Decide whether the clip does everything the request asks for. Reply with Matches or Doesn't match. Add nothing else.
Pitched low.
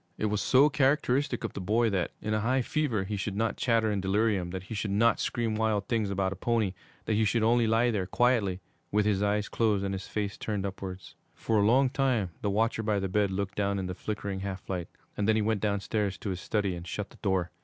Matches